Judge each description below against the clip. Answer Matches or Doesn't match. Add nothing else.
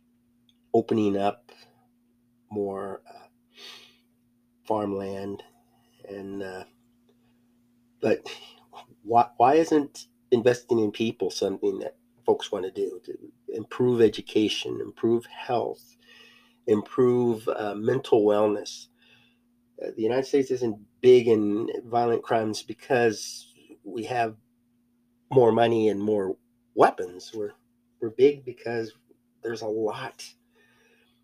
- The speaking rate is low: Matches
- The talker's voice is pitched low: Matches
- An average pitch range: Doesn't match